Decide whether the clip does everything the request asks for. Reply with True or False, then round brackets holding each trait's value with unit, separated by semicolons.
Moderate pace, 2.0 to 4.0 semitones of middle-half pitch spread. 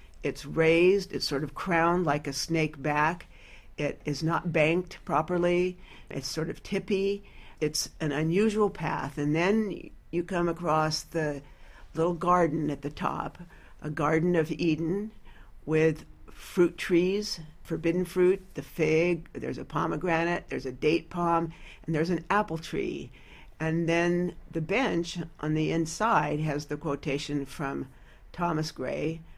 True (145 wpm; 2.6 semitones)